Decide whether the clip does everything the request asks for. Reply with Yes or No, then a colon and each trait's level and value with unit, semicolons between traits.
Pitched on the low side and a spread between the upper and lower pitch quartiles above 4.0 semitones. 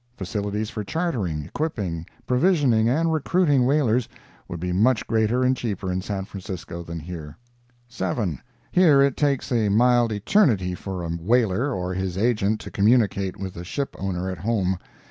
Yes: low, 105 Hz; wide, 5.5 semitones